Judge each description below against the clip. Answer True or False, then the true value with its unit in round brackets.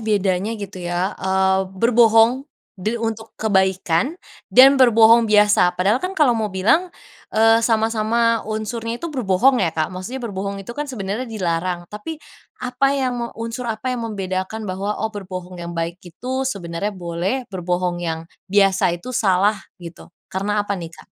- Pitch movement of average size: True (3.8 semitones)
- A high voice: True (210 Hz)